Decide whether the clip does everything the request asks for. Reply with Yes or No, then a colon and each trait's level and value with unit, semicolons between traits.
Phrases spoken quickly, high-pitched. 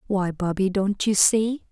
No: average, 175 wpm; high, 200 Hz